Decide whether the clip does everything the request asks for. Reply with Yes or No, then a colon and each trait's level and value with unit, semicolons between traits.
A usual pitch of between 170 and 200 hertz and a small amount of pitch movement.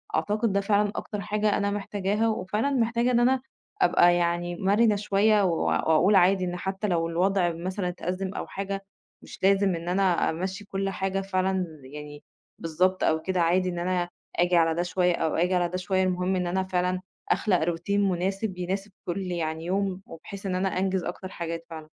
Yes: medium, 185 Hz; narrow, 2.2 semitones